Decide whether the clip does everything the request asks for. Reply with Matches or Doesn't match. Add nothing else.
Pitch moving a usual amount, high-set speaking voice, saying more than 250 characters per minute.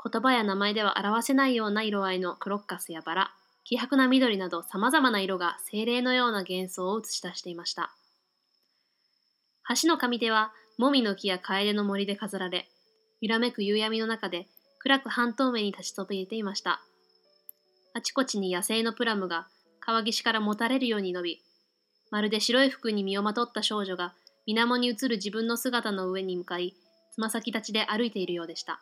Matches